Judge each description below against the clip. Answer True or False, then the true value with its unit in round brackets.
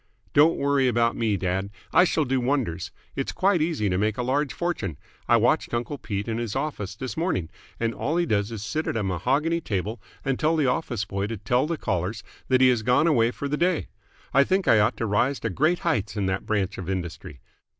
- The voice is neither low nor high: False (120 Hz)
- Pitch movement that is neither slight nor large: False (6.2 semitones)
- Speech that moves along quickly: True (225 wpm)